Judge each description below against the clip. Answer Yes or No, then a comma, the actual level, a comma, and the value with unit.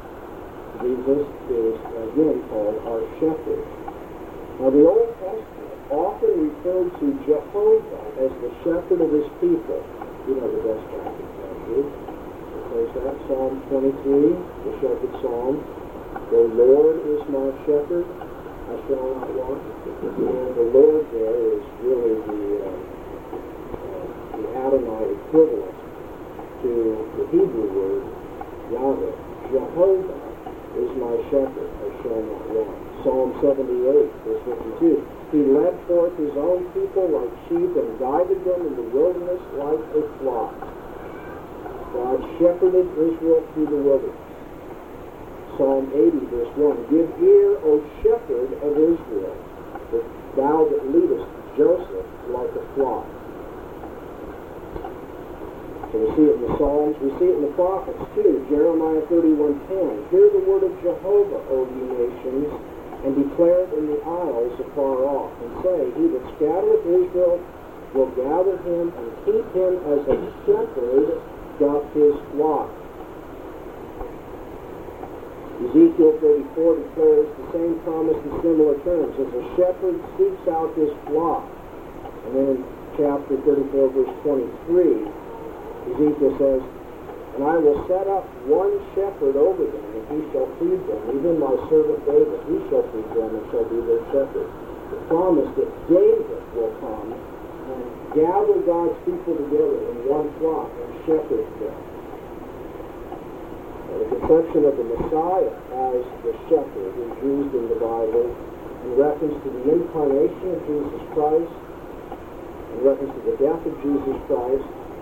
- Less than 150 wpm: Yes, slow, 135 wpm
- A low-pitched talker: No, very high, 380 Hz